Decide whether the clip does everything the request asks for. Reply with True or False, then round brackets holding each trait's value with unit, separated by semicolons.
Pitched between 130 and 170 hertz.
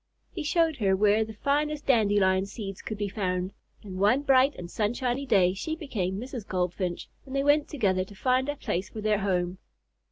False (210 Hz)